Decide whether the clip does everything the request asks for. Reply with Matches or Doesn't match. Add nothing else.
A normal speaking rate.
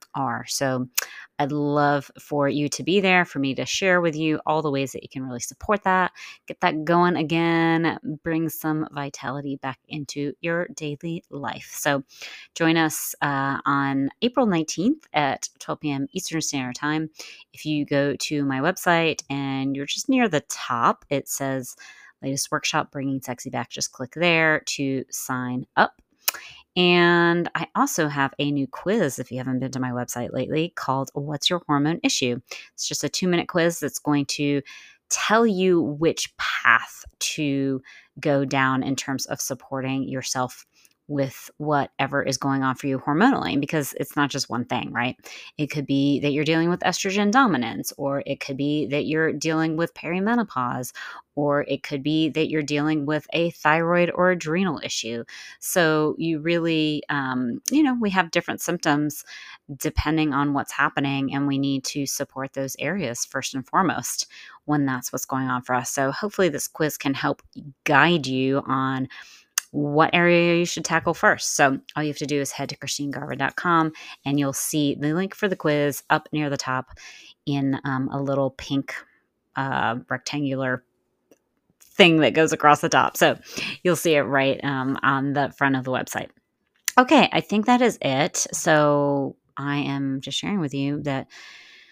Matches